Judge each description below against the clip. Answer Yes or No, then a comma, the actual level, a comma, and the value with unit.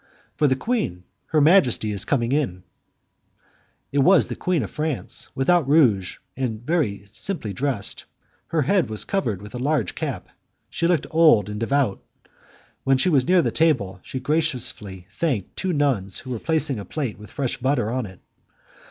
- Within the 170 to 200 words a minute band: Yes, average, 175 wpm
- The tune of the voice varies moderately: No, wide, 6.8 semitones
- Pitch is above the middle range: No, low, 130 Hz